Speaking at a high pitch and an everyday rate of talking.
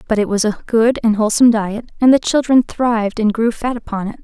No: high, 225 Hz; fast, 240 wpm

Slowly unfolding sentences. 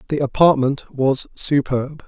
Yes: slow, 115 wpm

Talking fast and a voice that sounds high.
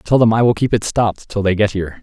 No: fast, 325 wpm; low, 105 Hz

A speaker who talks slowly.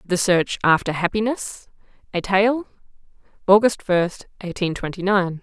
Yes: slow, 120 wpm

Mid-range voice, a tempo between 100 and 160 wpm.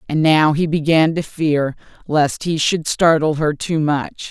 No: medium, 155 Hz; average, 180 wpm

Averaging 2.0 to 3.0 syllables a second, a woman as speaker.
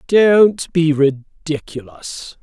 No: 2.6 syllables/s; male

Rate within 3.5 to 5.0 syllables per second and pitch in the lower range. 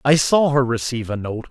No: 5.8 syllables/s; low, 130 Hz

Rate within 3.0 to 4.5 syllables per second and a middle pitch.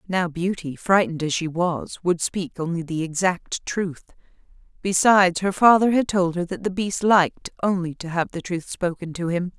No: 4.8 syllables/s; medium, 180 Hz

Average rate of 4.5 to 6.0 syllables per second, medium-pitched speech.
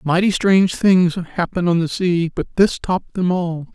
Yes: 4.6 syllables/s; medium, 175 Hz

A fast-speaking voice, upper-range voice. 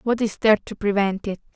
Yes: fast, 230 wpm; high, 210 Hz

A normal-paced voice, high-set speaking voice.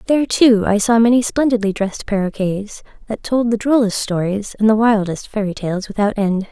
Yes: average, 185 wpm; high, 215 Hz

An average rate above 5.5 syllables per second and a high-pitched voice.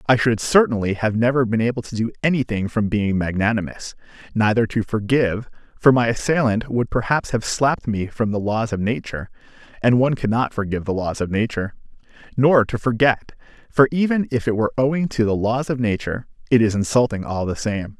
No: 5.8 syllables/s; low, 115 Hz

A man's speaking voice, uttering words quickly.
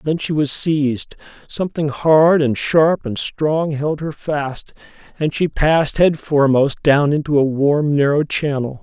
No: male; average, 165 wpm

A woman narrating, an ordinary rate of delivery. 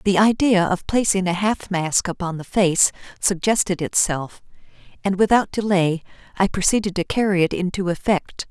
Yes: female; average, 155 wpm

